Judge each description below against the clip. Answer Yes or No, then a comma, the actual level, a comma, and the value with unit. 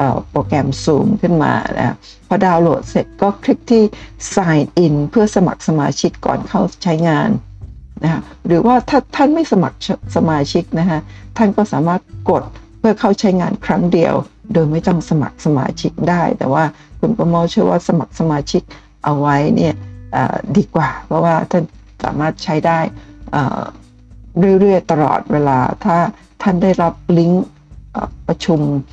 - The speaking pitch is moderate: Yes, medium, 170 Hz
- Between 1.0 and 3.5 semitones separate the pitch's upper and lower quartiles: No, average, 4.8 semitones